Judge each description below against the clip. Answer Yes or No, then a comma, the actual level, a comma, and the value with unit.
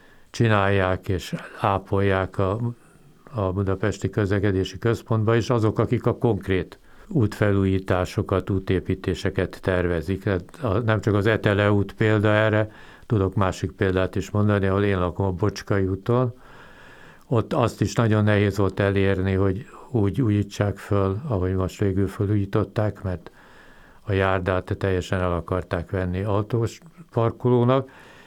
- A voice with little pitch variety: Yes, narrow, 2.3 semitones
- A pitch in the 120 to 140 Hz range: No, low, 100 Hz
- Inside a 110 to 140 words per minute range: Yes, average, 125 wpm